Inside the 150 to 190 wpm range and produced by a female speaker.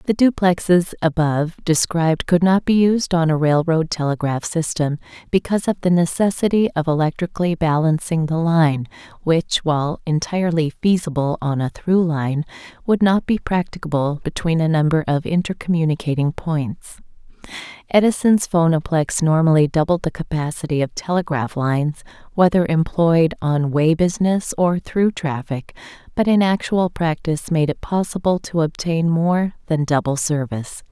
No: slow, 135 wpm; female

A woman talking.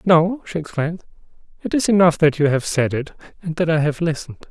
No: male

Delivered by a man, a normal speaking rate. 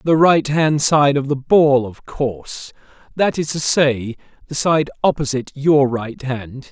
Yes: male; average, 150 wpm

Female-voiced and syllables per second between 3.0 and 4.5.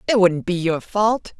Yes: female; 4.2 syllables/s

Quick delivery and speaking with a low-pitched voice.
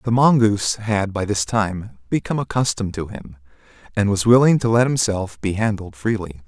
No: average, 175 wpm; low, 105 Hz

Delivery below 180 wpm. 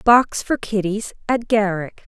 Yes: average, 140 wpm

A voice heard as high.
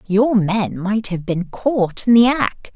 Yes: high, 210 Hz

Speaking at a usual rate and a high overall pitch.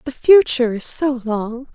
Yes: average, 170 wpm; very high, 255 Hz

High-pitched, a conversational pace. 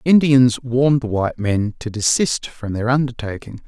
No: low, 120 Hz; average, 165 wpm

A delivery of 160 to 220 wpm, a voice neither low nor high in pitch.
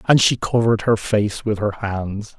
No: average, 200 wpm; low, 105 Hz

